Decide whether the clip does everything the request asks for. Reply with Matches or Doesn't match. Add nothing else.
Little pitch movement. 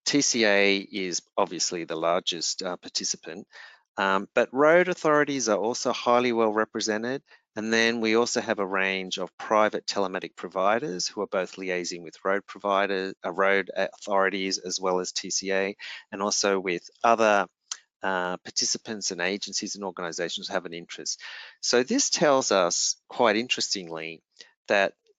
Doesn't match